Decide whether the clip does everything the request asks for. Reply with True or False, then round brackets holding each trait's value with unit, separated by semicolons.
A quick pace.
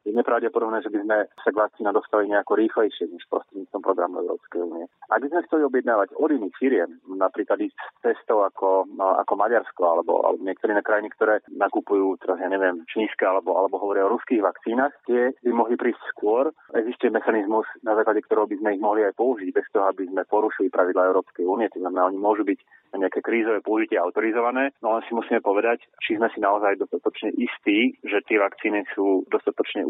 True (195 wpm)